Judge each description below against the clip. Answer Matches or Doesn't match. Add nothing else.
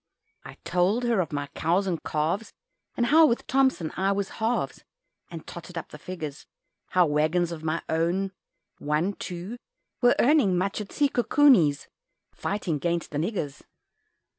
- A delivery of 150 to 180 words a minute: Matches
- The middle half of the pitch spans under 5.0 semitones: Doesn't match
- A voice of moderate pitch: Matches